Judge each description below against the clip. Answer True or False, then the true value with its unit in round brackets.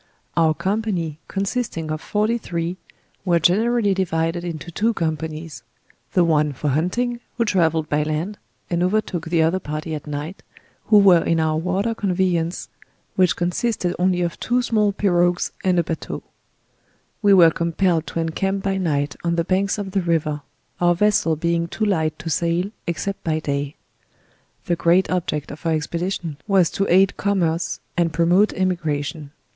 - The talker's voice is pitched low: False (175 Hz)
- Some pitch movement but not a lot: True (3.2 semitones)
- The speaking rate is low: False (165 wpm)